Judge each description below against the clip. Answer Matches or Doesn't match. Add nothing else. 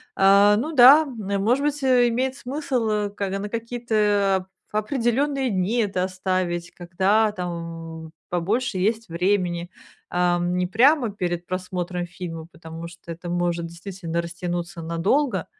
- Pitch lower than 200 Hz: Matches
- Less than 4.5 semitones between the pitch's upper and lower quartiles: Doesn't match